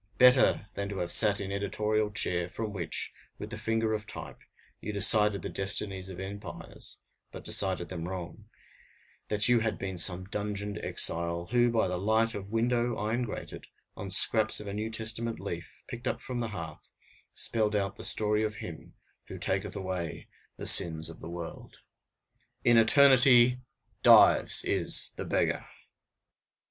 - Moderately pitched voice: No, low, 105 Hz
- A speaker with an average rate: Yes, average, 160 wpm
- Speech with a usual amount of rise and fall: Yes, average, 3.1 semitones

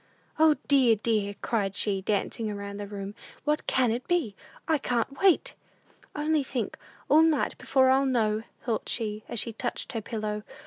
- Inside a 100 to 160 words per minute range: No, average, 170 wpm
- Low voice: No, high, 230 Hz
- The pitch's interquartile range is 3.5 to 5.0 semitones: Yes, average, 4.6 semitones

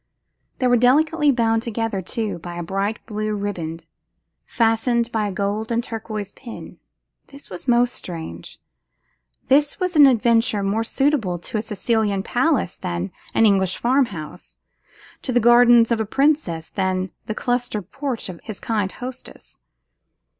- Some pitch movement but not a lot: Yes, average, 3.9 semitones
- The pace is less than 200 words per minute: Yes, average, 150 wpm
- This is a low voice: No, high, 225 Hz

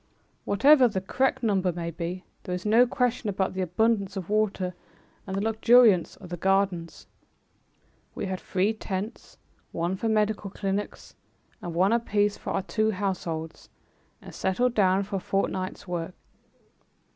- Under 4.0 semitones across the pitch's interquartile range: Yes, average, 2.8 semitones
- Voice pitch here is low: No, high, 195 Hz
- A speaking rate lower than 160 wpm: Yes, average, 150 wpm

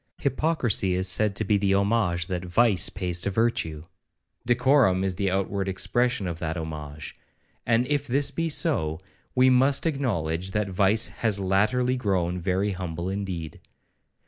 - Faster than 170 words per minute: No, average, 145 wpm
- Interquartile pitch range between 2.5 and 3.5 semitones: No, average, 5.2 semitones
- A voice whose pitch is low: Yes, very low, 95 Hz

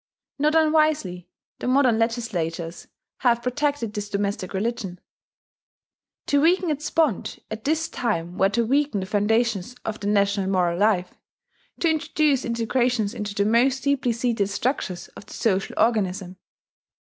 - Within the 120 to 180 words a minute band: Yes, average, 140 wpm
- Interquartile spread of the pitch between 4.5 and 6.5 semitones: Yes, average, 5.2 semitones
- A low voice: No, high, 225 Hz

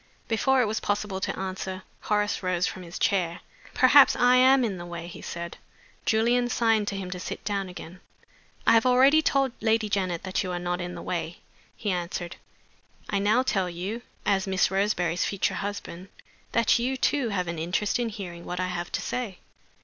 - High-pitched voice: Yes, high, 195 Hz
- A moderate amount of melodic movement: Yes, average, 4.2 semitones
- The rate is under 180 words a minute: No, average, 195 wpm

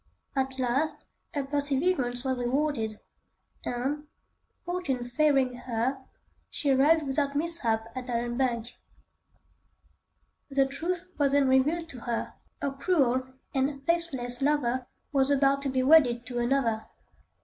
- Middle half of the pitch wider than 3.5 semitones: No, average, 2.9 semitones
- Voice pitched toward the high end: Yes, very high, 270 Hz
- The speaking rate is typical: No, slow, 120 wpm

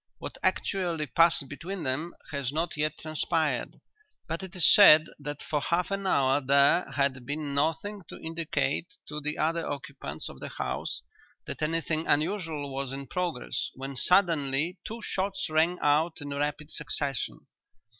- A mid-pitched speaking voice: Yes, medium, 155 Hz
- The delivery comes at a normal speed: Yes, average, 155 wpm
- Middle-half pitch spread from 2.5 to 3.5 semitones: Yes, average, 3.2 semitones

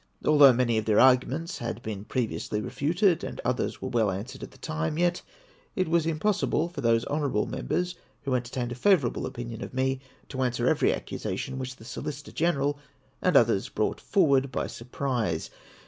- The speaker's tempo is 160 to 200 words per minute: Yes, average, 180 wpm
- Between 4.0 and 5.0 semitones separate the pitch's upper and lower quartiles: Yes, average, 4.4 semitones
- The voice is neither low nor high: No, low, 130 Hz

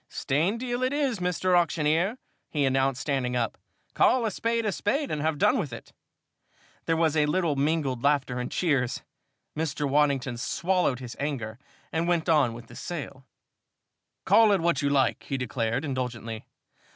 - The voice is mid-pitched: Yes, medium, 150 Hz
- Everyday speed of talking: Yes, average, 165 wpm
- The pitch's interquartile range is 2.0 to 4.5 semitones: No, average, 5.3 semitones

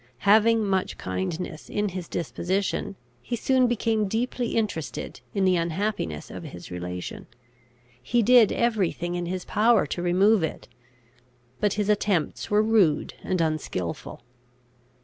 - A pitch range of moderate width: Yes, average, 4.4 semitones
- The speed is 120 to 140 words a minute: Yes, slow, 135 wpm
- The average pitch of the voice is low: No, high, 195 Hz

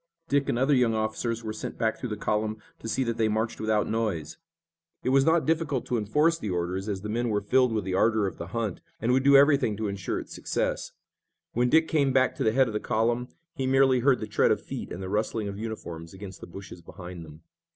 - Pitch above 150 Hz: No, low, 110 Hz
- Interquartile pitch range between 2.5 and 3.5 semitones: No, average, 4.2 semitones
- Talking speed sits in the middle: No, fast, 245 wpm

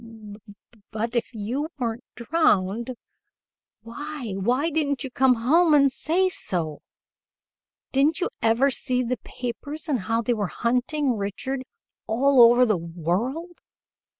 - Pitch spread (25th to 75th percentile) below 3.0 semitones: No, average, 4.1 semitones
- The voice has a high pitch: Yes, high, 245 Hz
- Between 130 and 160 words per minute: Yes, slow, 135 wpm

